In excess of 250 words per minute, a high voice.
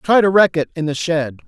No: fast, 285 wpm; medium, 170 Hz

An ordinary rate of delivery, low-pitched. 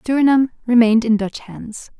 No: average, 150 wpm; high, 240 Hz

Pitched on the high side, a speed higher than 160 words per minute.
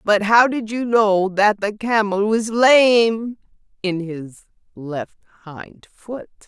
No: high, 210 Hz; average, 140 wpm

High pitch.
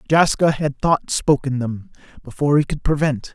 No: medium, 140 Hz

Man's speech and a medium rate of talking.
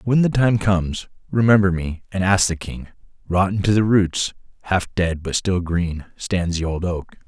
Yes: male; average, 190 wpm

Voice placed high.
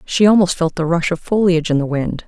No: medium, 170 Hz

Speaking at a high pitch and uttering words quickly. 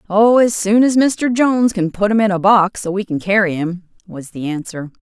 Yes: high, 200 Hz; fast, 240 wpm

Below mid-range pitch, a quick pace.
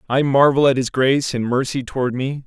Yes: low, 130 Hz; fast, 220 wpm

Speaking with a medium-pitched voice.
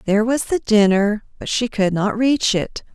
No: high, 220 Hz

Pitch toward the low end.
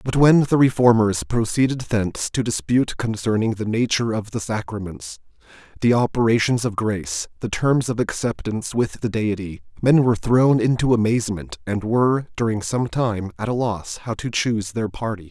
Yes: low, 115 Hz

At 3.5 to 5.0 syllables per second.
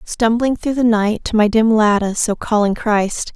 Yes: 4.6 syllables/s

